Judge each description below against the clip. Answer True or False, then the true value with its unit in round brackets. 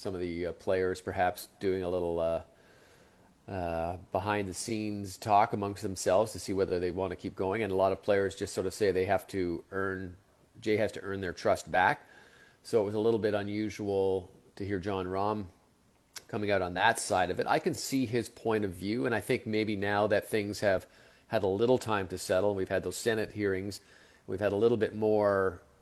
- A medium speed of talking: False (215 wpm)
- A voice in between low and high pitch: False (100 Hz)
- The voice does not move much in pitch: True (2.1 semitones)